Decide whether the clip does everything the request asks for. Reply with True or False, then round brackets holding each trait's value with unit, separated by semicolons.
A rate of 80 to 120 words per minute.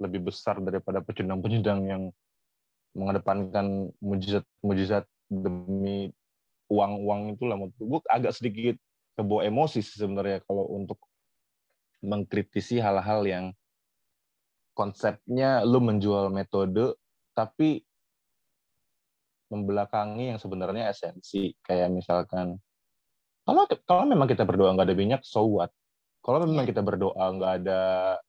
True (105 wpm)